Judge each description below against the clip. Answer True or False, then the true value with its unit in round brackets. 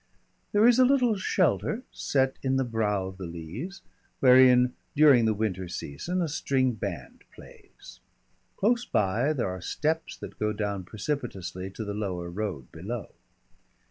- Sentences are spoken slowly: False (150 wpm)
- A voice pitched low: True (115 Hz)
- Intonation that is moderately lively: False (7.6 semitones)